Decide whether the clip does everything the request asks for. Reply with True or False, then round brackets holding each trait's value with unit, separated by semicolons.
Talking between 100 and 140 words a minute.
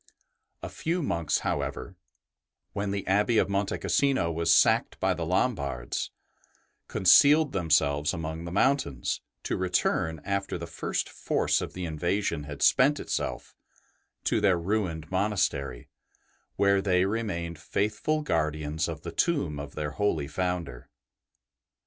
True (135 wpm)